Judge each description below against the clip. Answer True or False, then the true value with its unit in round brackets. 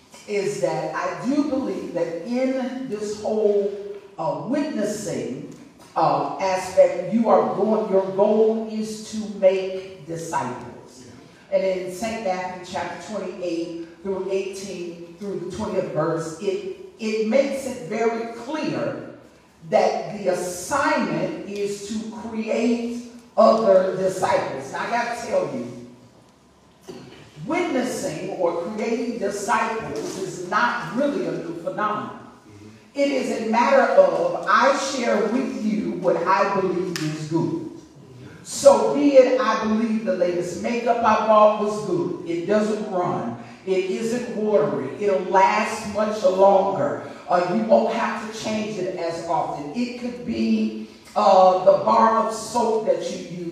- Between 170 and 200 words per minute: False (135 wpm)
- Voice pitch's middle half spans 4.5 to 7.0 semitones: False (4.1 semitones)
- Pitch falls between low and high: False (205 Hz)